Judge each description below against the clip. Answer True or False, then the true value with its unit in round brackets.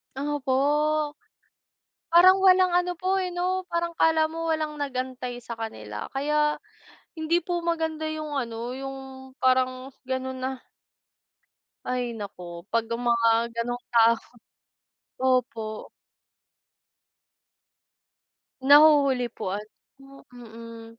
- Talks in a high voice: True (270 Hz)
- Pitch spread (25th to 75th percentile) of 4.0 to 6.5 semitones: True (4.6 semitones)